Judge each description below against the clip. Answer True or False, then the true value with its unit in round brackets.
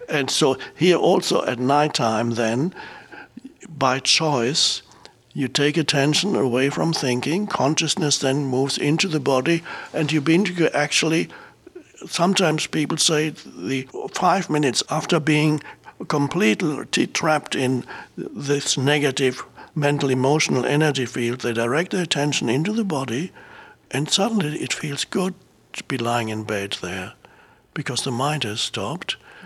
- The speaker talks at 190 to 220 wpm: False (135 wpm)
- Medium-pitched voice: True (145 Hz)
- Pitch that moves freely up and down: False (3.8 semitones)